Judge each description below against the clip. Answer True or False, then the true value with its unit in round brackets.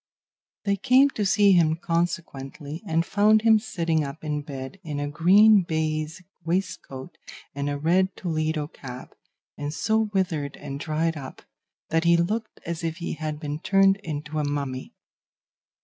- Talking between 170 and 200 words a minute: False (155 wpm)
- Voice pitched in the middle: True (160 Hz)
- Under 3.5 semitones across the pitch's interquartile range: False (4.3 semitones)